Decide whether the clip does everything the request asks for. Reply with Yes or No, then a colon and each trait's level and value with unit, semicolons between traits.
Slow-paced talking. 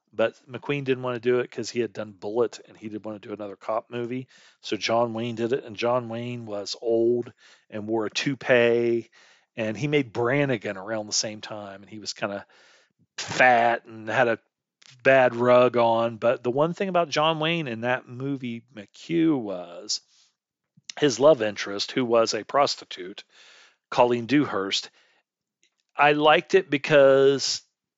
No: average, 170 wpm